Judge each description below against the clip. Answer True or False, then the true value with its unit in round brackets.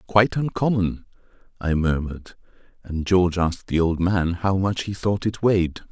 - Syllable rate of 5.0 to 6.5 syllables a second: True (5.2 syllables/s)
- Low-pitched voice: True (90 Hz)